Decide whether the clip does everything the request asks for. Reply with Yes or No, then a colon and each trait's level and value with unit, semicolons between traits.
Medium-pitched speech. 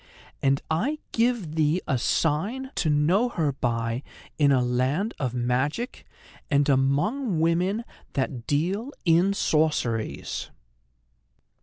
Yes: medium, 155 Hz